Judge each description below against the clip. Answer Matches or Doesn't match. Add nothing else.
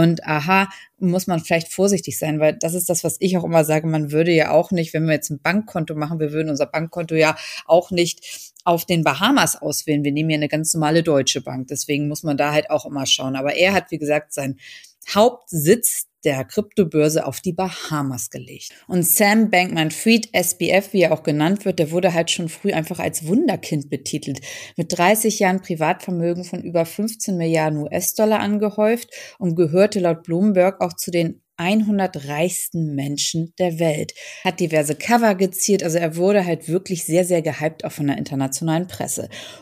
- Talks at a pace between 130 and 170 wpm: Doesn't match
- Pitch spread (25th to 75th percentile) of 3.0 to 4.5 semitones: Matches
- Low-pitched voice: Doesn't match